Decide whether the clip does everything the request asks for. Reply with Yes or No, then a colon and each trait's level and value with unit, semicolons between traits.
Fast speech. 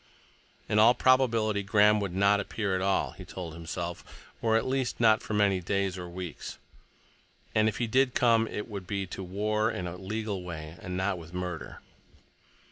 No: average, 180 wpm